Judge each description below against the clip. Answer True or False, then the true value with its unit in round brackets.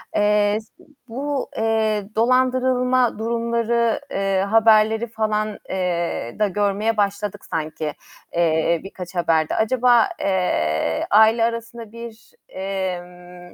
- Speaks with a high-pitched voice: True (215 Hz)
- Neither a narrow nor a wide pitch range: True (4.0 semitones)